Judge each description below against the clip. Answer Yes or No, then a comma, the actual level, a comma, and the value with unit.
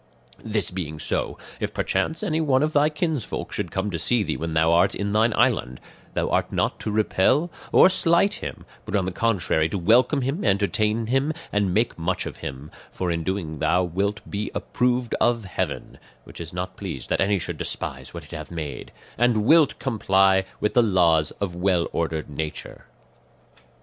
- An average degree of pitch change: No, wide, 5.8 semitones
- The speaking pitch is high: No, low, 100 Hz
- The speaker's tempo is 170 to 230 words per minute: Yes, average, 185 wpm